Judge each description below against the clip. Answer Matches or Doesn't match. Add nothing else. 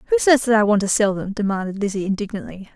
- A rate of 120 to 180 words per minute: Doesn't match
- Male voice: Doesn't match